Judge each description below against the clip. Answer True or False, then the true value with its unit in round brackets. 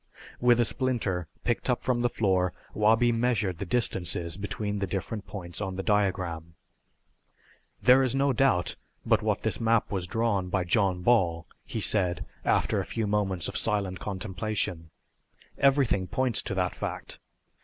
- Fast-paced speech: False (155 wpm)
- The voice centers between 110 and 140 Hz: False (100 Hz)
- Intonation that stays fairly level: False (4.3 semitones)